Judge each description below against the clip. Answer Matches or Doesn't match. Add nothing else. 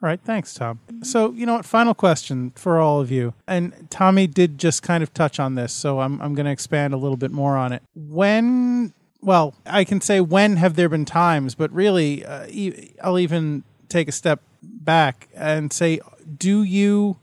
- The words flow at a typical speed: Matches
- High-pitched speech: Doesn't match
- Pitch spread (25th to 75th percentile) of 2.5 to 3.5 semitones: Doesn't match